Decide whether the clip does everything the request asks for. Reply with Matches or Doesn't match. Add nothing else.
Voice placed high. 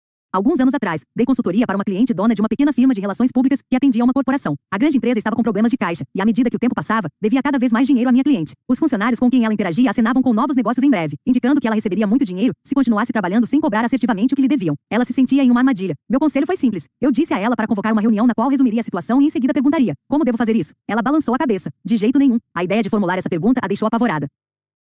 Matches